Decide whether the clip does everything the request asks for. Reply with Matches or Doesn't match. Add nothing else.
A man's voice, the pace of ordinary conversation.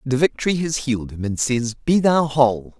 Matches